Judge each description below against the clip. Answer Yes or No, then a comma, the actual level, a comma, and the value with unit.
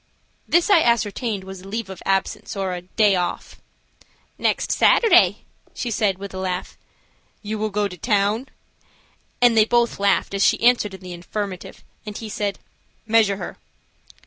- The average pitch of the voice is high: Yes, high, 205 Hz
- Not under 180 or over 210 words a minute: No, average, 165 wpm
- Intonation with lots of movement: No, average, 2.8 semitones